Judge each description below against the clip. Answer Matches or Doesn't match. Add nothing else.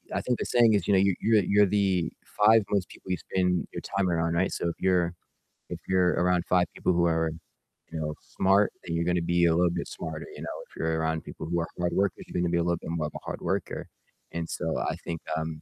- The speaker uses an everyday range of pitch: Doesn't match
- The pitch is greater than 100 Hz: Doesn't match